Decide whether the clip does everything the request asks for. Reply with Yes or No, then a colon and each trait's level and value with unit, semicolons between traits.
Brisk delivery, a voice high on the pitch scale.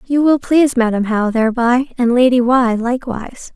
No: average, 170 wpm; high, 245 Hz